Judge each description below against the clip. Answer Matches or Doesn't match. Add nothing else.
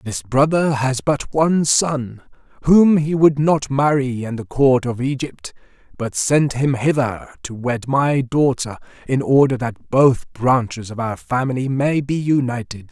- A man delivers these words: Matches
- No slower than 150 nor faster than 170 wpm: Matches